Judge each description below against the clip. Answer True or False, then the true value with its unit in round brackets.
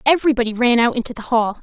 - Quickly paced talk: True (220 wpm)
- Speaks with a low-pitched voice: False (240 Hz)